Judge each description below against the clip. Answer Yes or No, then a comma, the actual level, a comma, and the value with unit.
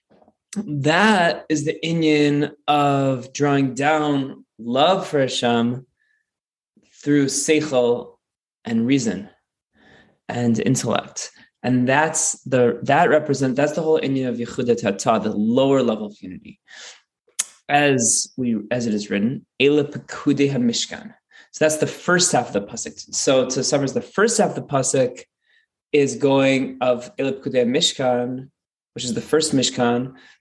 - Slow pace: Yes, slow, 130 wpm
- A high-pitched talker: No, medium, 140 Hz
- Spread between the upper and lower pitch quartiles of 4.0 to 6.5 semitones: No, average, 3.5 semitones